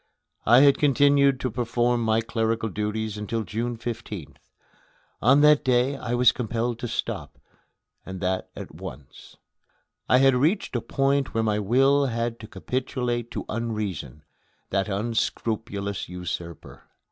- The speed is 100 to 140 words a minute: Yes, slow, 135 wpm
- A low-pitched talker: Yes, low, 115 Hz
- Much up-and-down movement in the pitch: No, average, 3.0 semitones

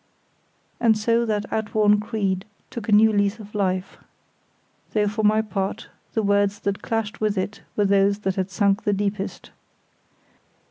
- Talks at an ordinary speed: Yes, average, 155 wpm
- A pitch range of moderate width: No, narrow, 1.5 semitones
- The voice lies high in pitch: Yes, high, 205 Hz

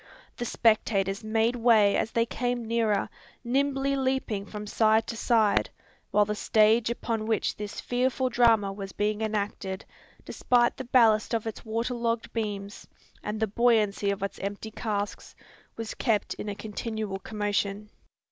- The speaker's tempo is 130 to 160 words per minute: Yes, average, 150 wpm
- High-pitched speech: Yes, high, 220 Hz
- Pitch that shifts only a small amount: Yes, narrow, 2.2 semitones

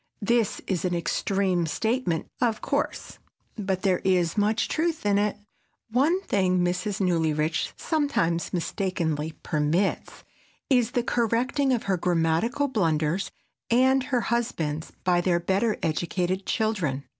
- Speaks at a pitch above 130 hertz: Yes, high, 190 Hz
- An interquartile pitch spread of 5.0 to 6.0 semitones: Yes, wide, 5.5 semitones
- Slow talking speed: Yes, slow, 125 wpm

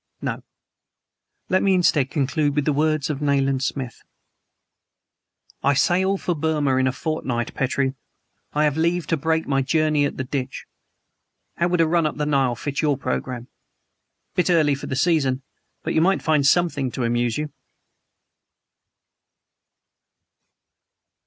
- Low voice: No, medium, 145 Hz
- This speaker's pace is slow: No, average, 145 wpm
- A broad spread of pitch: No, average, 3.1 semitones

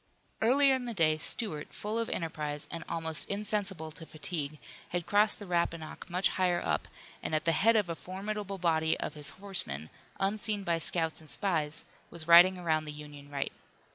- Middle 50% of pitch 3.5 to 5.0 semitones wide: Yes, average, 4.3 semitones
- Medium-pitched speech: Yes, medium, 170 Hz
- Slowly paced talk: No, average, 180 wpm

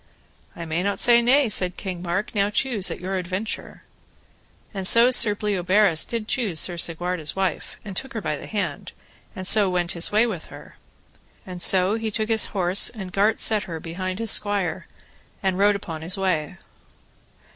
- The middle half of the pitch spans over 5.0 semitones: No, average, 3.2 semitones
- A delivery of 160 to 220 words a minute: Yes, average, 180 wpm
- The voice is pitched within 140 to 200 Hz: Yes, high, 190 Hz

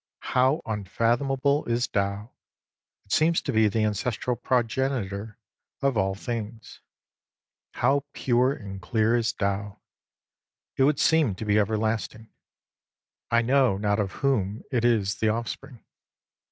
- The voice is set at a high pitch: No, low, 115 Hz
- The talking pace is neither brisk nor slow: No, slow, 130 wpm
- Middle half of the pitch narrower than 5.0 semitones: Yes, average, 4.0 semitones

